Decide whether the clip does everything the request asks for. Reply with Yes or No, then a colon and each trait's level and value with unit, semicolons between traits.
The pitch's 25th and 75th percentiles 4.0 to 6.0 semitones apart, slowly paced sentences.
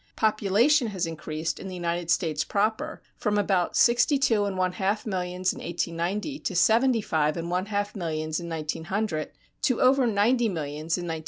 No: average, 4.6 semitones; average, 180 wpm